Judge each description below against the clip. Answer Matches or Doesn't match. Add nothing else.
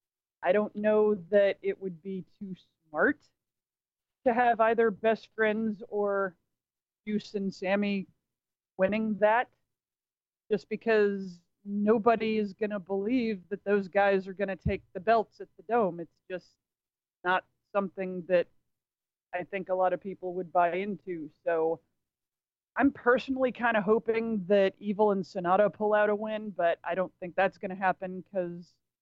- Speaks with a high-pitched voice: Matches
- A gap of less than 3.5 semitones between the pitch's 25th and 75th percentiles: Matches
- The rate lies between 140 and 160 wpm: Matches